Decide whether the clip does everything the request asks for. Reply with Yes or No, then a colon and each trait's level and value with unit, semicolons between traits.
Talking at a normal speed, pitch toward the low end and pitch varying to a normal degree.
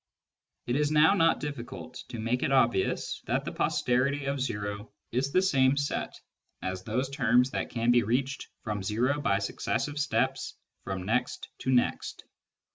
Yes: average, 160 wpm; low, 125 Hz; average, 3.5 semitones